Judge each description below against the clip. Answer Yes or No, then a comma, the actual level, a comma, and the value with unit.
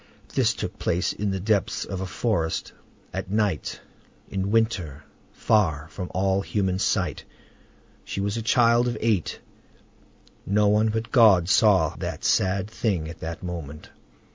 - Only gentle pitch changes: No, average, 3.6 semitones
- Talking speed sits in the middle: Yes, average, 145 wpm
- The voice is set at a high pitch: No, low, 100 Hz